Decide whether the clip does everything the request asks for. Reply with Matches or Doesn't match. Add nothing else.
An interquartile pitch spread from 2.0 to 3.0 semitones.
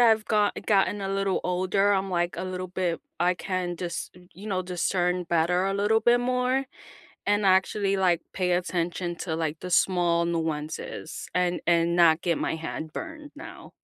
Matches